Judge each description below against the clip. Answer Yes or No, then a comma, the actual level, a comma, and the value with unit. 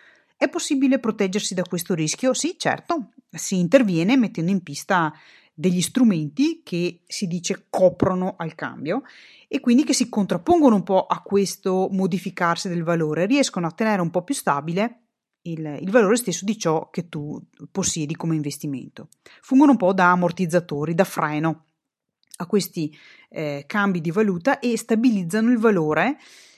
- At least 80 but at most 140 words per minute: No, average, 155 wpm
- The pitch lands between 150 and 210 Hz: Yes, high, 190 Hz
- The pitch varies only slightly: No, wide, 5.5 semitones